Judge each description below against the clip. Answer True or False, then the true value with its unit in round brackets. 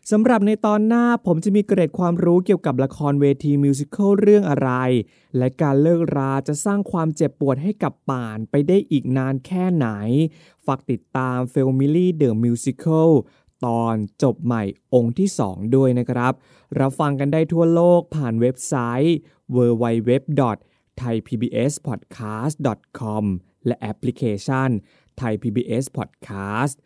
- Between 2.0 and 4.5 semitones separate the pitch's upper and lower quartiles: False (5.2 semitones)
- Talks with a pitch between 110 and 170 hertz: True (135 Hz)